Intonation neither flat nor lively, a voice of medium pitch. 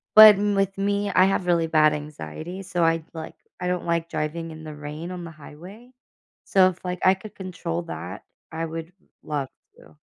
Yes: average, 3.2 semitones; medium, 170 Hz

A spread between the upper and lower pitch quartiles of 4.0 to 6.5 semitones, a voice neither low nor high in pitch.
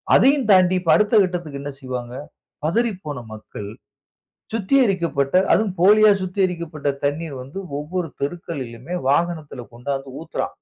Yes: average, 5.1 semitones; medium, 165 Hz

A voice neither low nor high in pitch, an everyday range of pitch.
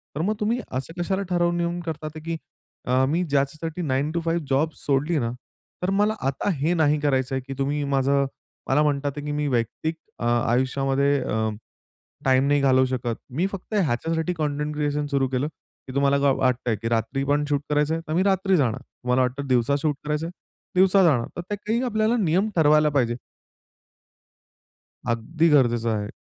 Yes: medium, 145 Hz; average, 3.9 semitones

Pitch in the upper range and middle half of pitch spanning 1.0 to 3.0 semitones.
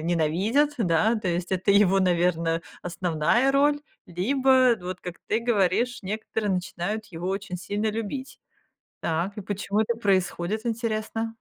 No: high, 200 Hz; average, 4.2 semitones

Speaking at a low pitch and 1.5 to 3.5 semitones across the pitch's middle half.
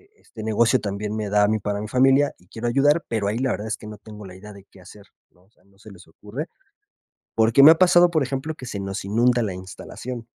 No: low, 110 Hz; average, 4.1 semitones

